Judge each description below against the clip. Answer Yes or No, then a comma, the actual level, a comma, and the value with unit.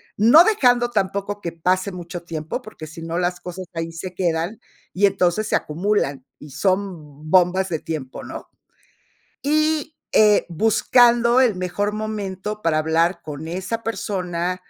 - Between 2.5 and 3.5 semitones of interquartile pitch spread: No, average, 4.2 semitones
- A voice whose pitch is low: No, medium, 185 Hz